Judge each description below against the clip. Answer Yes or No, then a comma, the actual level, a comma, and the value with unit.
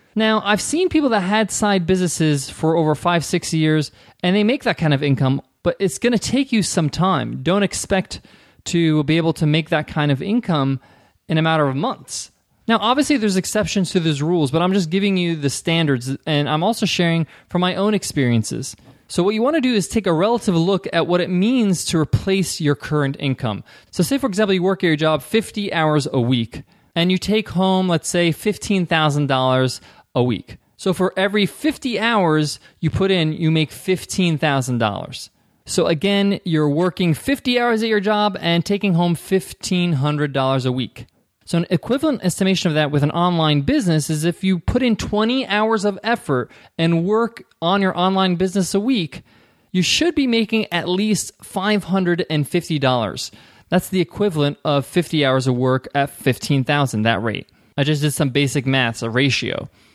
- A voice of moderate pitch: Yes, medium, 170 Hz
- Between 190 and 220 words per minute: Yes, average, 195 wpm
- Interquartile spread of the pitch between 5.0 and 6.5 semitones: Yes, wide, 5.4 semitones